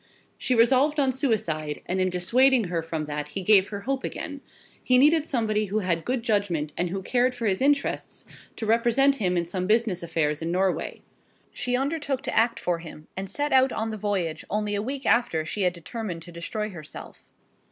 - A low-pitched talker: No, high, 210 Hz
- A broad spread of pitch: Yes, wide, 6.4 semitones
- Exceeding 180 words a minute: Yes, average, 200 wpm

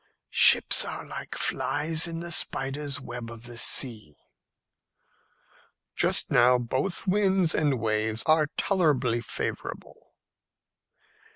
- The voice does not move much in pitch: No, wide, 5.6 semitones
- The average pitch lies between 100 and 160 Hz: Yes, low, 135 Hz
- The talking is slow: Yes, slow, 105 wpm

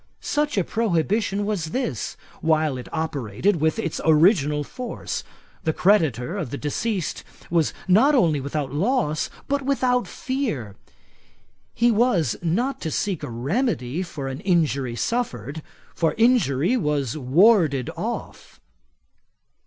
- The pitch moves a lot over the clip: Yes, wide, 7.8 semitones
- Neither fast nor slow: No, slow, 125 wpm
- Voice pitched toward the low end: No, medium, 165 Hz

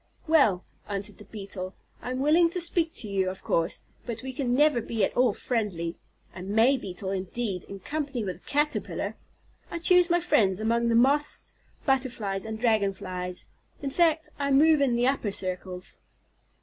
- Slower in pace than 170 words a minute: No, average, 175 wpm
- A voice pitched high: Yes, high, 235 Hz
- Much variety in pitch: Yes, wide, 6.4 semitones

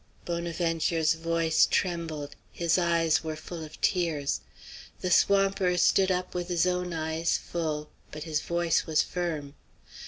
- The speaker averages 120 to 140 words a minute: Yes, slow, 135 wpm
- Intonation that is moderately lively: No, narrow, 1.9 semitones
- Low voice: No, medium, 165 Hz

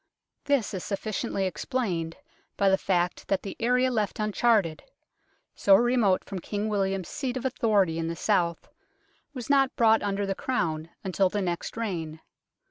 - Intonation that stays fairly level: No, average, 4.3 semitones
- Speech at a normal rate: Yes, average, 160 wpm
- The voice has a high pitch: Yes, high, 200 Hz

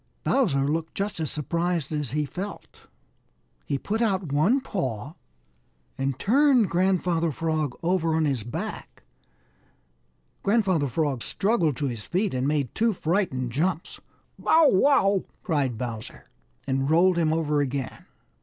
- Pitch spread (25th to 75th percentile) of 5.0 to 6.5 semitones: Yes, wide, 5.6 semitones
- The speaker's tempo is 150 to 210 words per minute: No, slow, 135 wpm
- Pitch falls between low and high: Yes, medium, 160 Hz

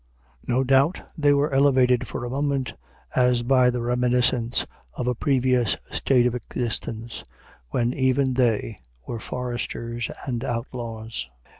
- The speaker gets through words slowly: Yes, slow, 130 wpm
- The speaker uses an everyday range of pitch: No, narrow, 1.8 semitones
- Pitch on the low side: Yes, low, 125 Hz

